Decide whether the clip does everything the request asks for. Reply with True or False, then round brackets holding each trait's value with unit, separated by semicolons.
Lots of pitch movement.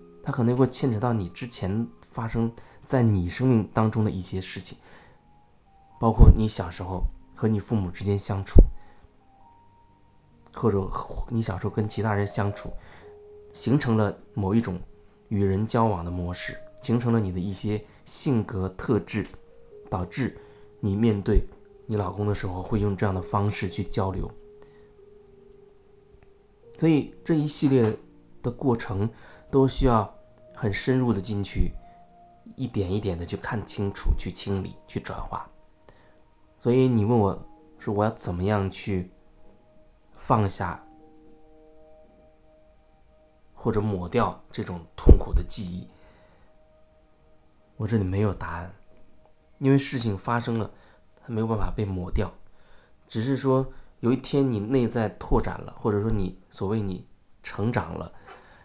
False (5.0 semitones)